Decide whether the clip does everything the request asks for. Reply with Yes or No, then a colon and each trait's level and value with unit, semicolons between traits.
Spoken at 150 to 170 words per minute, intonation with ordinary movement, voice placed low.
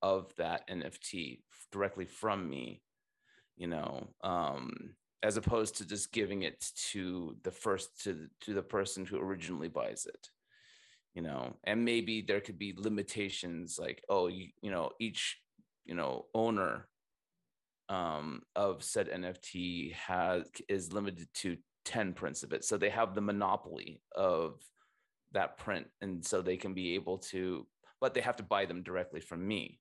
Yes: average, 160 wpm; average, 3.1 semitones; very low, 95 Hz